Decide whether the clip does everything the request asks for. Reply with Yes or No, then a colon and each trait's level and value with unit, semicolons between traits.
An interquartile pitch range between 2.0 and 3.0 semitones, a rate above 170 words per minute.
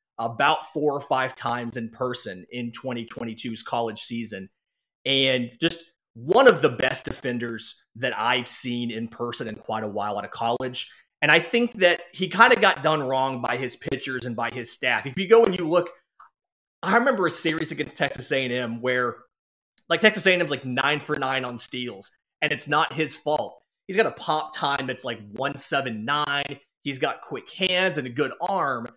No: average, 4.8 semitones; average, 190 wpm